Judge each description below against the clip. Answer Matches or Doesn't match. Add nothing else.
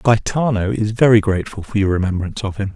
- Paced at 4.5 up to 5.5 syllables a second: Doesn't match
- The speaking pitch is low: Matches